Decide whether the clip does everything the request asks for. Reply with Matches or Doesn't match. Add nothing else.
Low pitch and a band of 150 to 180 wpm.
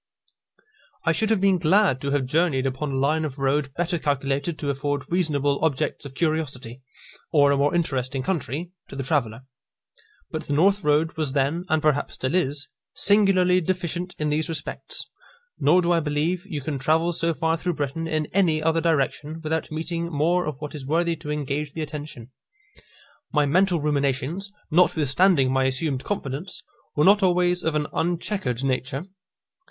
Doesn't match